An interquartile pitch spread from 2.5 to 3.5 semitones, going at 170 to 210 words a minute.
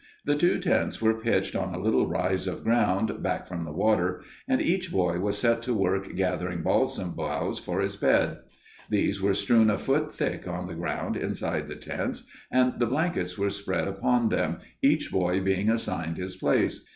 No: average, 4.1 semitones; average, 190 wpm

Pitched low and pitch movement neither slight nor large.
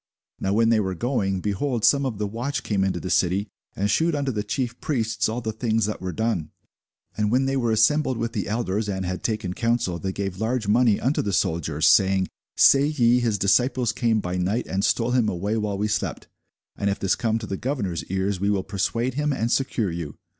Yes: low, 110 Hz; average, 3.8 semitones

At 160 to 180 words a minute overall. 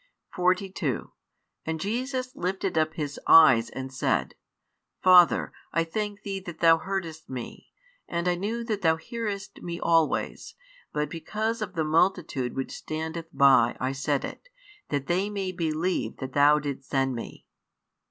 No: average, 150 wpm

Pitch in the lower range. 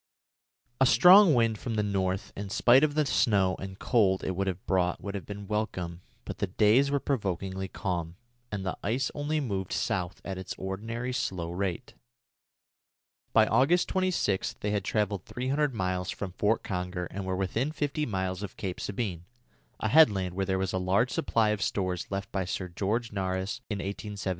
Yes: low, 100 Hz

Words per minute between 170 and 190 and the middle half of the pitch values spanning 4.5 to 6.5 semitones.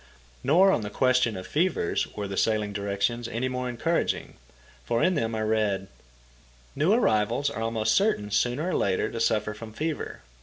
Yes: average, 175 wpm; average, 5.0 semitones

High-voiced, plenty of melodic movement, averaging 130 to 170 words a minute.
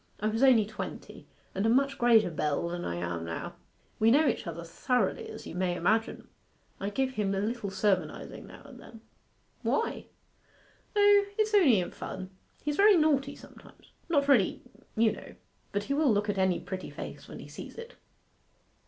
No: high, 220 Hz; wide, 6.9 semitones; average, 180 wpm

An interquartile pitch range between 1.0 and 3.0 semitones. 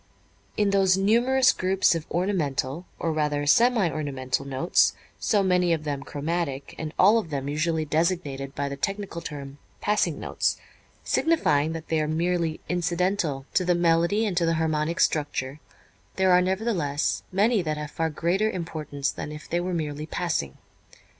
No: average, 3.8 semitones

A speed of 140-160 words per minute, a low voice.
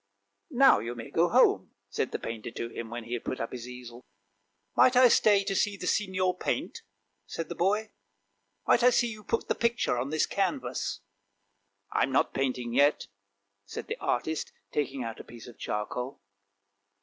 No: average, 195 wpm; low, 125 Hz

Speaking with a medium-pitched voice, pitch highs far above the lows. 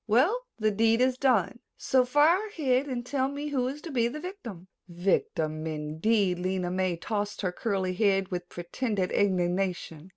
No: high, 215 Hz; wide, 6.2 semitones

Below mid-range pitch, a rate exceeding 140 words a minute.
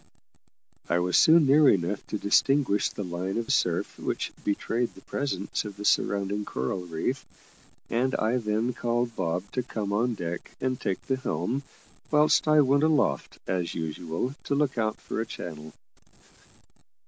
Yes: low, 110 Hz; average, 160 wpm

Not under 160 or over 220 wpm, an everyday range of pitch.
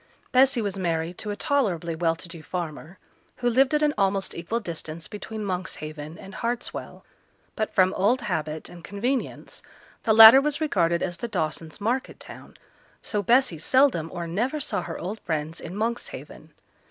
No: average, 165 wpm; wide, 5.9 semitones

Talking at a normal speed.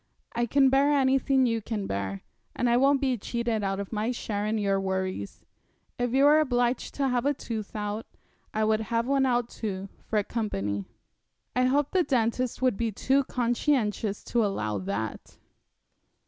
Yes: average, 175 wpm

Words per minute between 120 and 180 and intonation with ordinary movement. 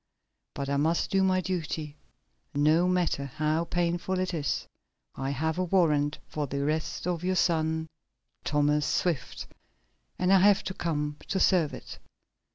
Yes: average, 150 wpm; average, 3.5 semitones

